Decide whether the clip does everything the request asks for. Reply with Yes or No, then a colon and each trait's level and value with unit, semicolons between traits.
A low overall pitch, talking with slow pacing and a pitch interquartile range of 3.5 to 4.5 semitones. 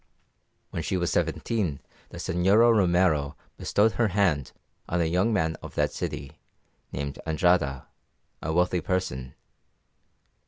Yes: very low, 90 Hz; slow, 125 wpm; average, 4.1 semitones